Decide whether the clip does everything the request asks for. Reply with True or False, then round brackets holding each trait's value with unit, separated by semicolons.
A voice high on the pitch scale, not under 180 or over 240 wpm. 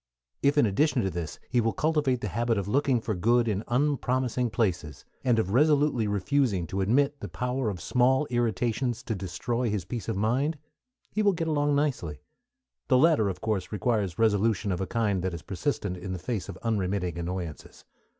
False (115 Hz; 190 wpm)